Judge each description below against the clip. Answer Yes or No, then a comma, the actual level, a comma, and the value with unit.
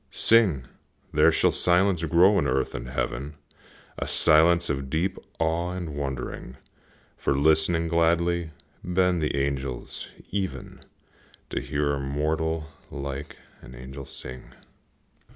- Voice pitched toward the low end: Yes, very low, 80 Hz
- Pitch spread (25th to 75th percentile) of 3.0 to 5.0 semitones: Yes, average, 4.0 semitones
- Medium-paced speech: No, slow, 120 wpm